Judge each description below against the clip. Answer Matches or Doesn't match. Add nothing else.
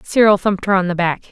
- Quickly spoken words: Matches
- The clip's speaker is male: Doesn't match